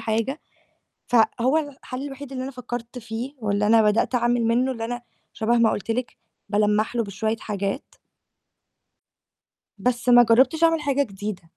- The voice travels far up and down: No, average, 2.9 semitones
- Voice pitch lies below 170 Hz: No, high, 235 Hz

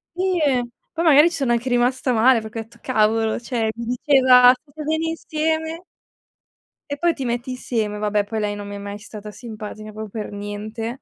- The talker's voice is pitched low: No, high, 240 Hz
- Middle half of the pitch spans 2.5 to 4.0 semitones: No, average, 4.9 semitones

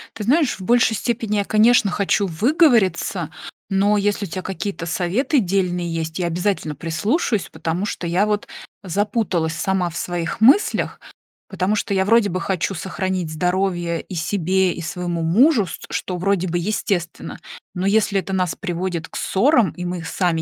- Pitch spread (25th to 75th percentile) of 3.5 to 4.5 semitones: No, average, 3.1 semitones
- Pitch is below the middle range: No, high, 190 Hz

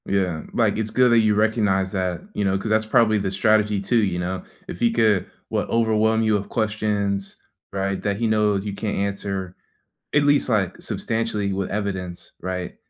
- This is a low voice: Yes, low, 105 Hz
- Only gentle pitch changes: Yes, narrow, 2.2 semitones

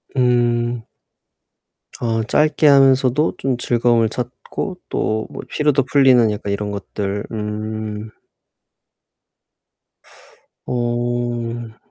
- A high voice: No, low, 120 Hz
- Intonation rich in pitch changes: No, narrow, 2.6 semitones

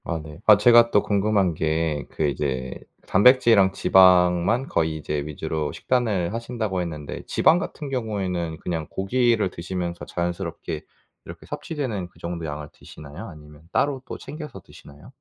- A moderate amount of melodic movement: No, wide, 6.0 semitones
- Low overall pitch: Yes, very low, 90 Hz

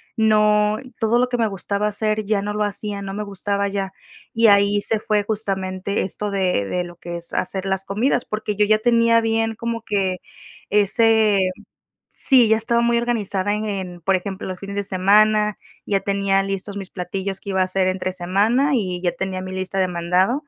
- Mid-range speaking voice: No, high, 200 Hz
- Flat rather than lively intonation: Yes, narrow, 2.2 semitones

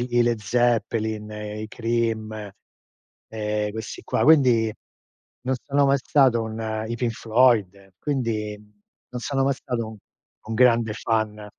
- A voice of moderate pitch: No, low, 115 Hz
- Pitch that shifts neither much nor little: No, narrow, 2.3 semitones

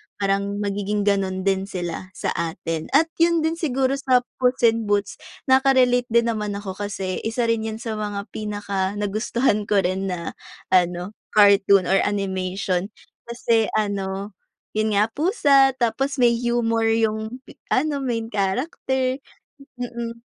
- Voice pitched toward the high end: Yes, high, 215 Hz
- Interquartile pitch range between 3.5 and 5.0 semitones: Yes, average, 3.9 semitones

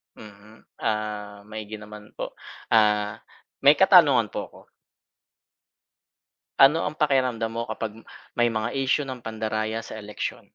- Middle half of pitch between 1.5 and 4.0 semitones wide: Yes, average, 3.3 semitones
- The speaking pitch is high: No, low, 110 Hz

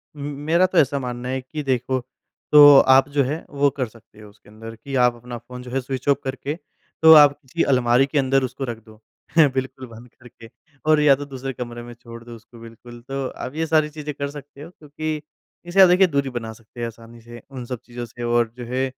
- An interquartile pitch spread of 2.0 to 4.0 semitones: Yes, average, 3.2 semitones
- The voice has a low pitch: Yes, low, 130 Hz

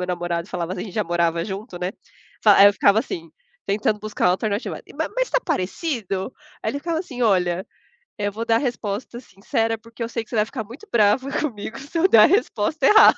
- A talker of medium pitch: No, high, 215 Hz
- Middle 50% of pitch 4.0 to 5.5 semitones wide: Yes, average, 4.6 semitones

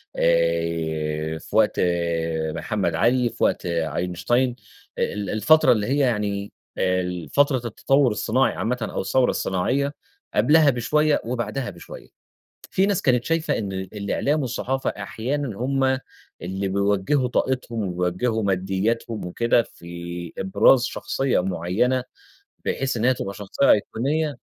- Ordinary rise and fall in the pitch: No, wide, 6.0 semitones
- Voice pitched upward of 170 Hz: No, low, 110 Hz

